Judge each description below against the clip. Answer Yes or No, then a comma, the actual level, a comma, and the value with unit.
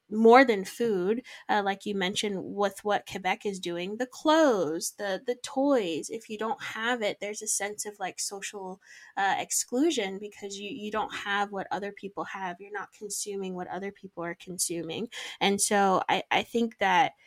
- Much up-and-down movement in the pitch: No, average, 2.8 semitones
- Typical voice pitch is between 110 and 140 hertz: No, high, 205 Hz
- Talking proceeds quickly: No, average, 185 wpm